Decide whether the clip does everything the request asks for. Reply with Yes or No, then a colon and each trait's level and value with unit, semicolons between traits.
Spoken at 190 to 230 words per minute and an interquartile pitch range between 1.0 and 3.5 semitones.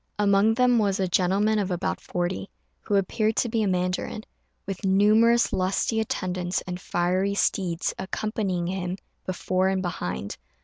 No: average, 145 wpm; average, 2.7 semitones